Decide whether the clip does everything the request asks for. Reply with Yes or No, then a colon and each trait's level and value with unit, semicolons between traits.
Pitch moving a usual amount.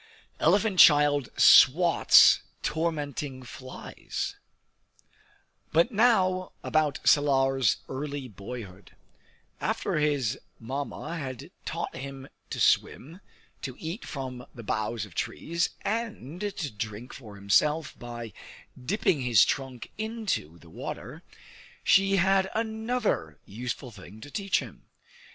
No: wide, 6.7 semitones